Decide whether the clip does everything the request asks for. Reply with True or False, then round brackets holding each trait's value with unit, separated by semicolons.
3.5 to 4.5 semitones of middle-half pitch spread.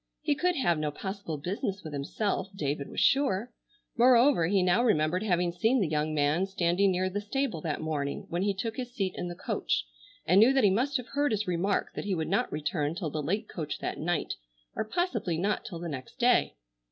False (5.6 semitones)